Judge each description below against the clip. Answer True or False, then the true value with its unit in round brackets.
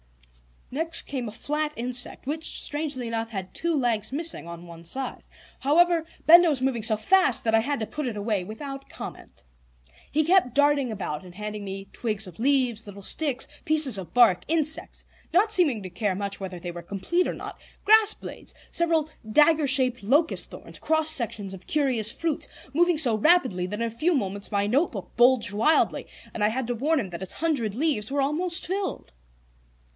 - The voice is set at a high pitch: True (255 Hz)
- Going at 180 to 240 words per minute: True (190 wpm)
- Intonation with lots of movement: True (6.8 semitones)